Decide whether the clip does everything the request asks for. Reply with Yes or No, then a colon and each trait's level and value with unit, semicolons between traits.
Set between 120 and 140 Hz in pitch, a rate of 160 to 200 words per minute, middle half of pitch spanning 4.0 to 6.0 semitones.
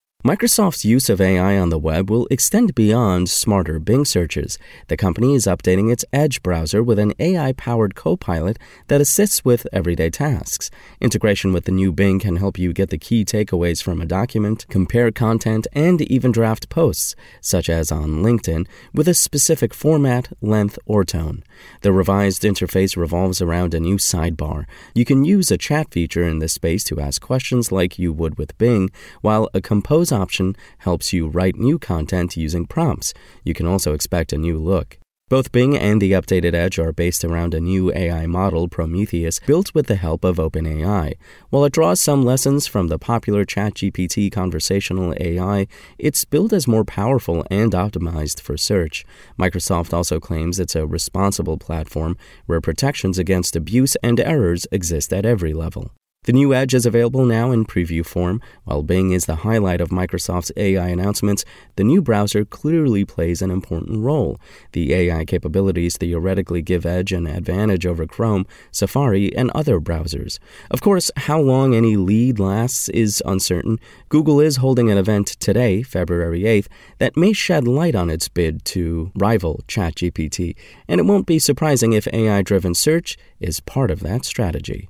No: very low, 95 Hz; average, 170 wpm; wide, 5.5 semitones